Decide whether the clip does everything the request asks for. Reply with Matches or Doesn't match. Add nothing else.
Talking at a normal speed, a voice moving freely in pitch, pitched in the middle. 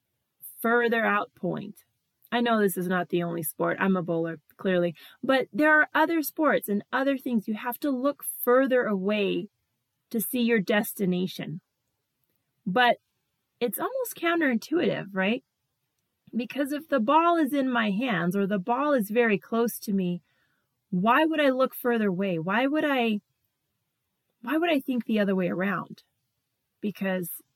Doesn't match